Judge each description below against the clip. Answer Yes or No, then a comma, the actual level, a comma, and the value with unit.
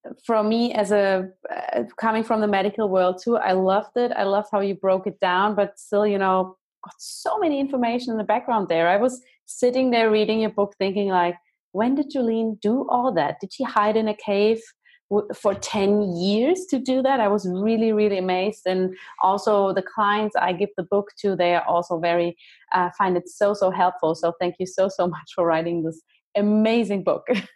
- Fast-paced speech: Yes, fast, 210 wpm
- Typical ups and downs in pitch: Yes, average, 3.2 semitones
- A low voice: No, high, 205 Hz